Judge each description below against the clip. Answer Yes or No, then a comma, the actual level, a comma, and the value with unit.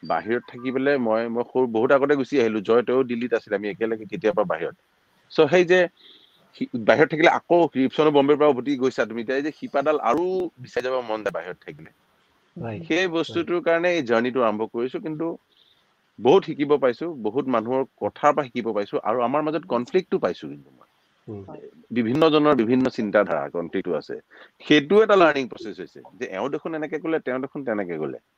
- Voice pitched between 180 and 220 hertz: No, medium, 140 Hz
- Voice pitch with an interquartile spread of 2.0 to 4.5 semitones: No, average, 5.3 semitones